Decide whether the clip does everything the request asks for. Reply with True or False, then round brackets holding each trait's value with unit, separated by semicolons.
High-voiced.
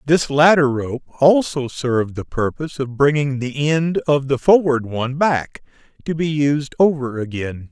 False (140 Hz)